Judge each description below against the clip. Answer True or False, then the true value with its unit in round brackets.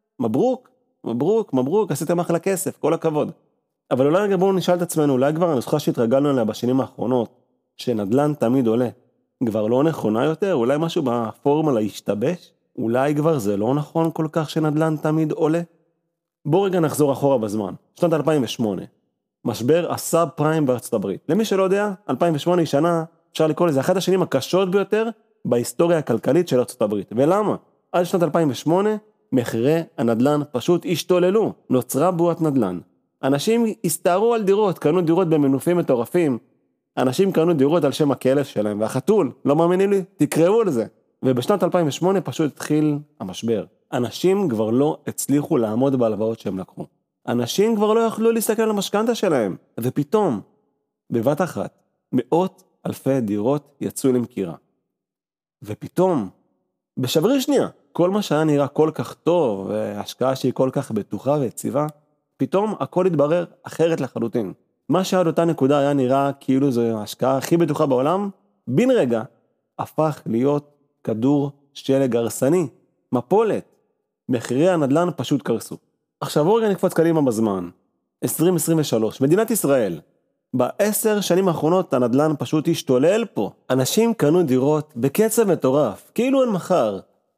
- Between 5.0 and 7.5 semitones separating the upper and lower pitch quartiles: True (5.4 semitones)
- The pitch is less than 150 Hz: False (155 Hz)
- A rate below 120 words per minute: False (140 wpm)